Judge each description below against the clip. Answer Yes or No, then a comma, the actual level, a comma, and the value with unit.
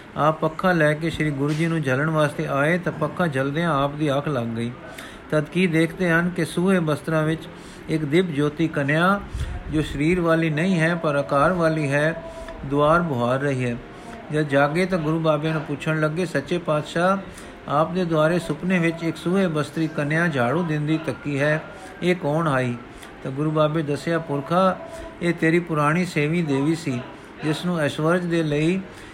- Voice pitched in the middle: Yes, medium, 155 Hz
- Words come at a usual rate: No, fast, 175 wpm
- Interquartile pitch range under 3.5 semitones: Yes, average, 2.8 semitones